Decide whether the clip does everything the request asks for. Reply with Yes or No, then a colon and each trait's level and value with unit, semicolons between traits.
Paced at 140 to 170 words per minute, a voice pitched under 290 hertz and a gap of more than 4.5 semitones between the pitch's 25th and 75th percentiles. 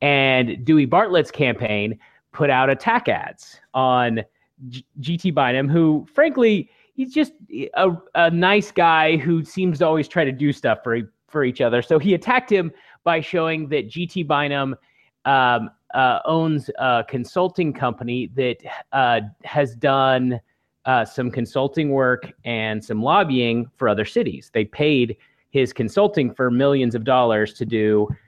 Yes: average, 150 wpm; medium, 140 Hz; average, 5.3 semitones